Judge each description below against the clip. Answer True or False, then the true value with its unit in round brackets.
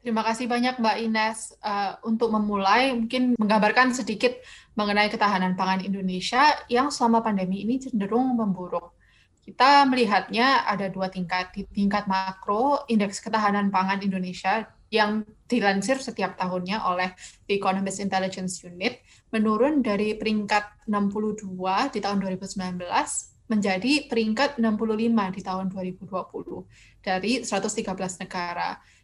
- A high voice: True (210 Hz)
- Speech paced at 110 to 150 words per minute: True (120 wpm)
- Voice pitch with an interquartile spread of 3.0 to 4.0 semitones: True (3.3 semitones)